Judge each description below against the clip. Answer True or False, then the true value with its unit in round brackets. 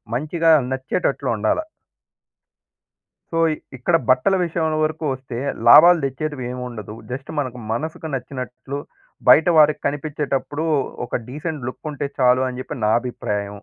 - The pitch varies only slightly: False (3.5 semitones)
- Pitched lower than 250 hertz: True (135 Hz)